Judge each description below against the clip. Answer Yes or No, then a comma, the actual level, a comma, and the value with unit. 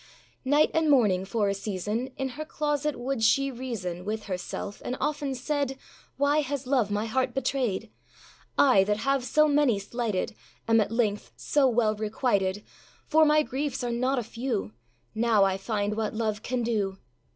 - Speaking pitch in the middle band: No, high, 235 Hz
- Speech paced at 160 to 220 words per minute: Yes, average, 170 wpm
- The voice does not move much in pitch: No, average, 4.6 semitones